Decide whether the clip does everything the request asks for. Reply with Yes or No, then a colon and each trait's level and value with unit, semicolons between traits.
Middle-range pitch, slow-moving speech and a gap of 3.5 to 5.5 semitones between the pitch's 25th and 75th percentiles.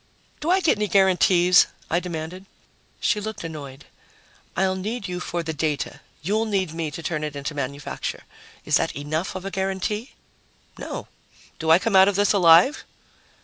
No: medium, 180 Hz; average, 170 wpm; average, 3.9 semitones